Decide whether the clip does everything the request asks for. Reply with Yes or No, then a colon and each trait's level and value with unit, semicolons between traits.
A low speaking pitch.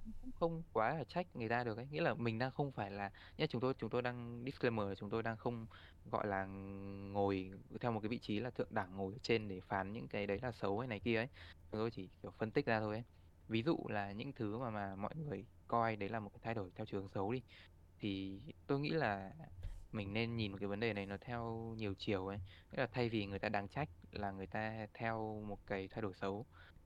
Yes: low, 105 Hz